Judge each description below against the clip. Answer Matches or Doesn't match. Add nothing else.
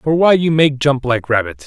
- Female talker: Doesn't match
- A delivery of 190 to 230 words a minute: Doesn't match